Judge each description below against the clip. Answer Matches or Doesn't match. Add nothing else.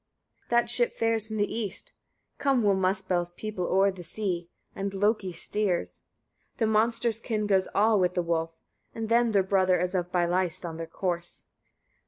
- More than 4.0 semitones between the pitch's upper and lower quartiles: Doesn't match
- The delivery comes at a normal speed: Matches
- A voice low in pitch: Doesn't match